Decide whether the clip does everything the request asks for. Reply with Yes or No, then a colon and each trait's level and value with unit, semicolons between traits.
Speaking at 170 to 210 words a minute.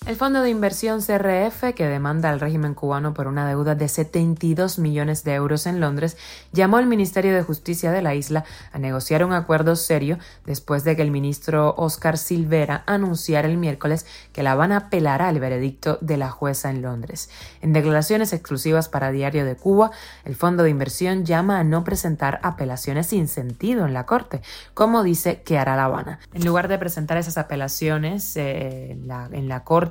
Yes: average, 185 wpm